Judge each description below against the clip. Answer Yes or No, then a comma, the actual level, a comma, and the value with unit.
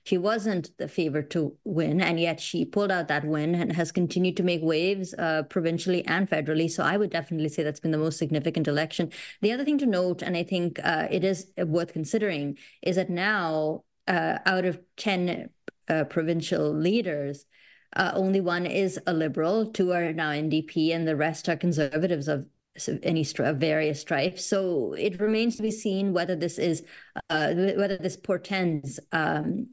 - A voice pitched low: No, medium, 175 Hz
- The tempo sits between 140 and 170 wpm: No, average, 185 wpm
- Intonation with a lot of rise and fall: No, average, 3.1 semitones